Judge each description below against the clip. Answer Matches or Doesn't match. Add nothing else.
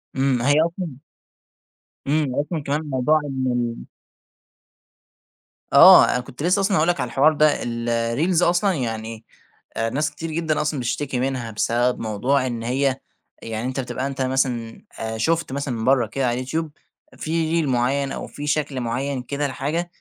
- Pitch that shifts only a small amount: Doesn't match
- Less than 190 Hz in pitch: Matches